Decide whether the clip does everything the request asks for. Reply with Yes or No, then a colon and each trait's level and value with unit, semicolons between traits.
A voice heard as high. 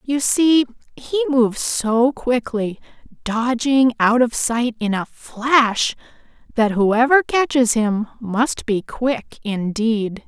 Yes: high, 240 Hz